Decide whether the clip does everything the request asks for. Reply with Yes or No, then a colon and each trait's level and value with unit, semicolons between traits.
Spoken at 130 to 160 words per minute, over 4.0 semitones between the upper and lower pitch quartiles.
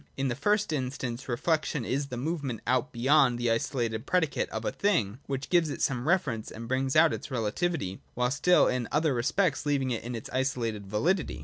No: average, 195 wpm; average, 4.5 semitones